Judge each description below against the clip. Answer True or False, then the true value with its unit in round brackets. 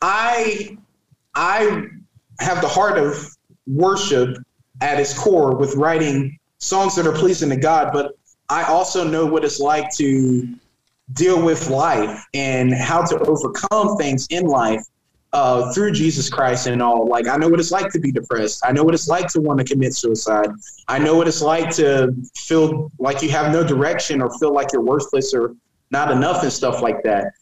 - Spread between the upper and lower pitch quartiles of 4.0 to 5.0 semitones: True (4.3 semitones)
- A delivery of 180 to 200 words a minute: True (185 wpm)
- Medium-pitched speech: True (150 Hz)